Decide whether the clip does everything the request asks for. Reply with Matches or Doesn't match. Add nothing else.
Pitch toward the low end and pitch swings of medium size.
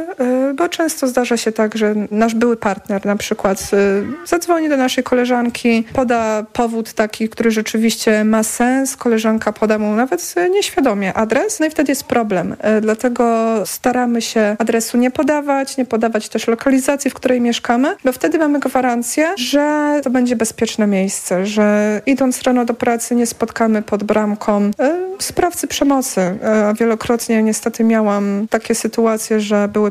Doesn't match